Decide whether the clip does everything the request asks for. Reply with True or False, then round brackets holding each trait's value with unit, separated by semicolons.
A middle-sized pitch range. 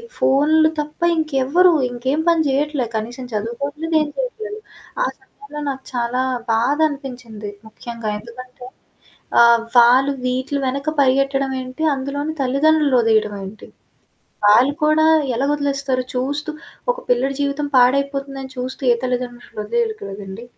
True (3.2 semitones)